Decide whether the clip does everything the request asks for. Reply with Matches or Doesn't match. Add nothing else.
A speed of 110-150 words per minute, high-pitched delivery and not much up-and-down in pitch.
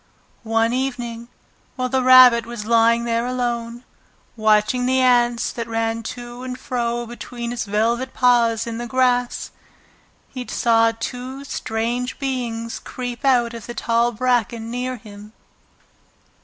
Matches